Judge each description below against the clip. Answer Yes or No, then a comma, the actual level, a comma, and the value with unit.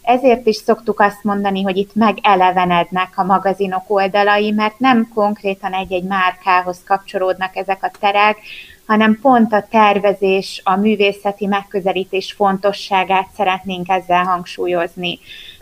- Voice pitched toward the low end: No, high, 195 Hz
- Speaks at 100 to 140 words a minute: Yes, average, 120 wpm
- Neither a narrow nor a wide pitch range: No, narrow, 1.6 semitones